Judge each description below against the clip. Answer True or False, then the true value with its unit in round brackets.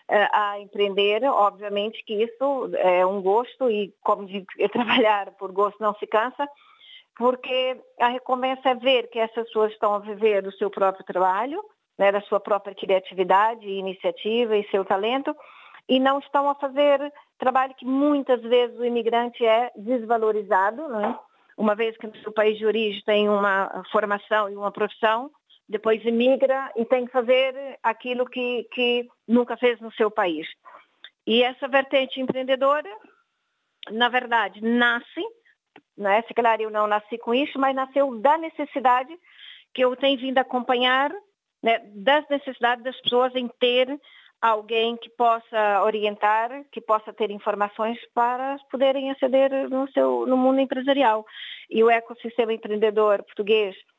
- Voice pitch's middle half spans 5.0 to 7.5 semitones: False (3.9 semitones)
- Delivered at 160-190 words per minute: False (150 wpm)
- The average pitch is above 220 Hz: True (235 Hz)